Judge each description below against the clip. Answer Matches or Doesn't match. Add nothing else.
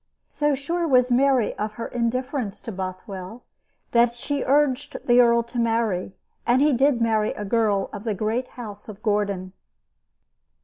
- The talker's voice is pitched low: Doesn't match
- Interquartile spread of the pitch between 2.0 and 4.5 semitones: Matches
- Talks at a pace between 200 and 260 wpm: Doesn't match